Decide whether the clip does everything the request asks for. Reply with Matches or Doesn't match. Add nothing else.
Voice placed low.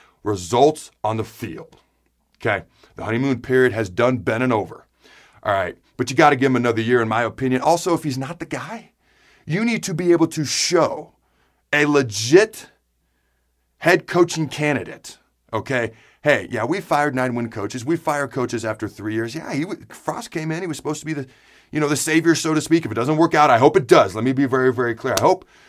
Matches